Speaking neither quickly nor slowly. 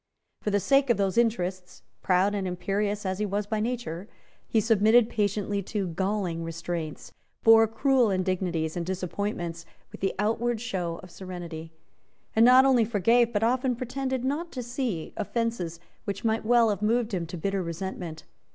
Yes: average, 165 wpm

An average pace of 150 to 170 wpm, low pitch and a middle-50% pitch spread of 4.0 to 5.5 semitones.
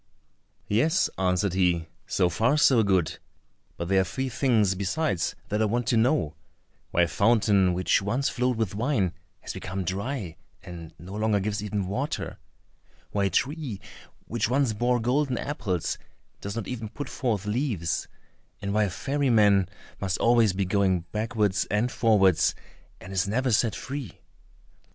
Yes: average, 160 wpm; low, 105 Hz; average, 4.4 semitones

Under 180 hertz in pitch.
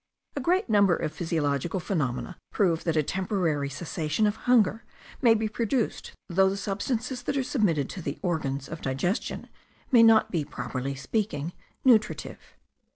No: medium, 185 Hz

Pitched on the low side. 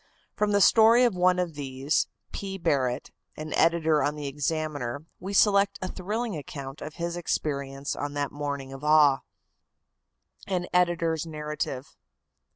No: medium, 155 Hz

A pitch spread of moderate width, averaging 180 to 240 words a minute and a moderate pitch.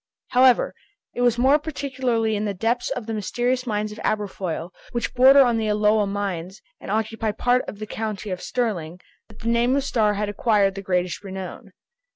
No: average, 3.4 semitones; average, 190 wpm; high, 215 Hz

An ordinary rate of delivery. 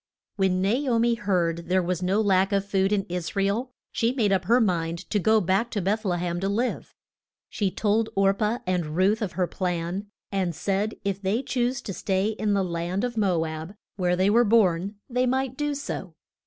No: fast, 215 wpm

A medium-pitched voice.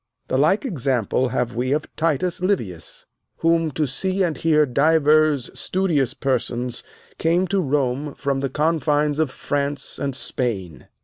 Yes: medium, 145 Hz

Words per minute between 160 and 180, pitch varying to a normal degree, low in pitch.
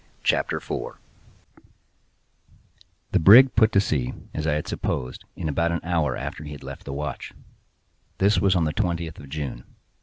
Yes: average, 170 wpm; average, 3.3 semitones; very low, 80 Hz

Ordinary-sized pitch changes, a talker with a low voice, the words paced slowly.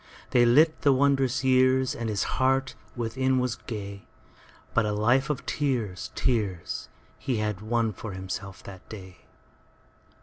Yes: average, 3.9 semitones; low, 120 Hz; slow, 125 wpm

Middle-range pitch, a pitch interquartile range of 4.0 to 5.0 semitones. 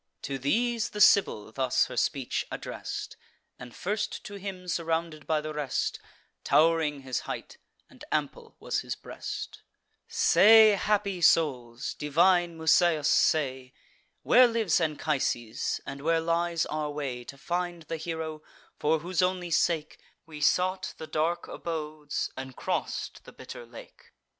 No: medium, 160 Hz; average, 3.6 semitones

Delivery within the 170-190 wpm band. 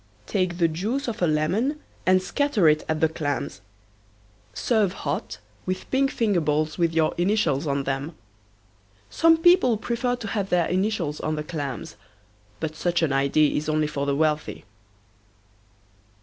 No: average, 155 wpm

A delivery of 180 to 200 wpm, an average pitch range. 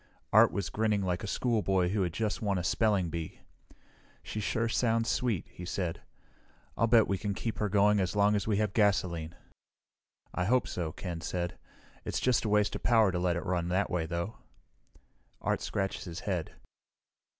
Yes: average, 185 wpm; average, 3.4 semitones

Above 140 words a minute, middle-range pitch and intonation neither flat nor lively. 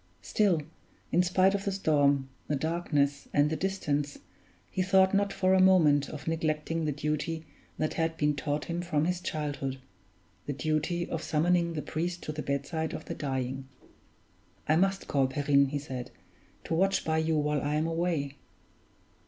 Yes: average, 170 wpm; medium, 155 Hz; average, 3.2 semitones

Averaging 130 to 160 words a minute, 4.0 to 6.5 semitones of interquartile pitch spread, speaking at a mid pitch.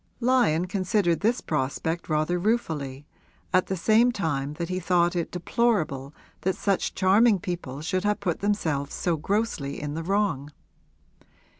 Yes: average, 145 wpm; average, 5.0 semitones; medium, 175 Hz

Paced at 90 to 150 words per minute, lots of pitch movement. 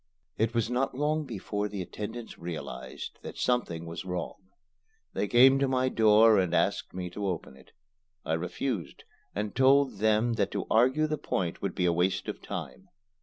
No: average, 175 wpm; wide, 6.0 semitones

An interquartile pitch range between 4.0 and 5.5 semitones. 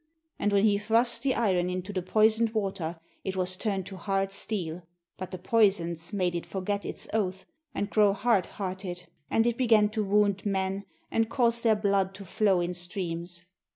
No: average, 2.8 semitones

